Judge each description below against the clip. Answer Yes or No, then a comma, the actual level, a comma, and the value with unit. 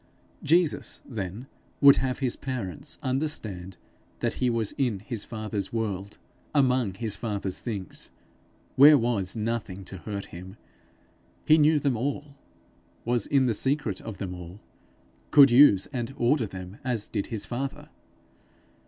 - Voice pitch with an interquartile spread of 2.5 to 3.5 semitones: No, average, 5.2 semitones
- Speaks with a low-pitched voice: Yes, low, 115 Hz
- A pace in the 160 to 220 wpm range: No, average, 140 wpm